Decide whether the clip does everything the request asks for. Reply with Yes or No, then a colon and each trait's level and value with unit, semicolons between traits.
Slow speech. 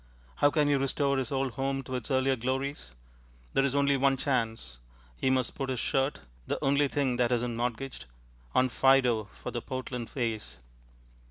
No: average, 175 wpm